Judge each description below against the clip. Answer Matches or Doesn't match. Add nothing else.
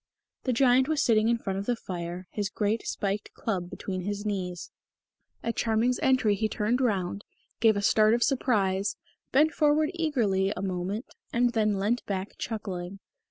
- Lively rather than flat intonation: Doesn't match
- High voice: Matches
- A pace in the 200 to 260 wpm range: Doesn't match